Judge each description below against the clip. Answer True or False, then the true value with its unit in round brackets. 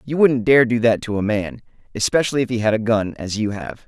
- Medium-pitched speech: False (115 Hz)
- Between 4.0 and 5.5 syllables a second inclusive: False (5.8 syllables/s)